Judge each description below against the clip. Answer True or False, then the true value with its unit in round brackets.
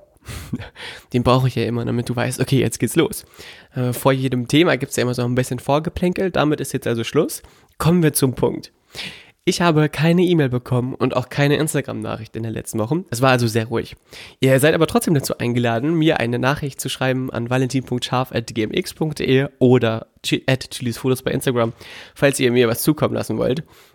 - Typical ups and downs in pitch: True (3.2 semitones)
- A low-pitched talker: True (130 Hz)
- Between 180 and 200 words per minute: True (190 wpm)